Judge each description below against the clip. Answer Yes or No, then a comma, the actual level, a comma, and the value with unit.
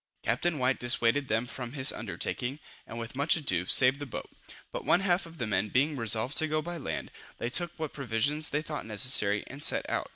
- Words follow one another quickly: Yes, fast, 215 wpm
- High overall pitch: No, low, 130 Hz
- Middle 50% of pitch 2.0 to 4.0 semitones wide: No, average, 4.7 semitones